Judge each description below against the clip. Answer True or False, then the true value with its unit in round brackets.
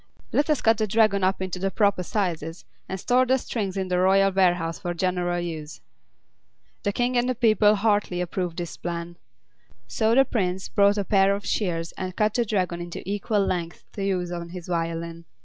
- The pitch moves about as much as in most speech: True (3.1 semitones)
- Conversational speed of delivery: True (195 wpm)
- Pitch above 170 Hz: True (190 Hz)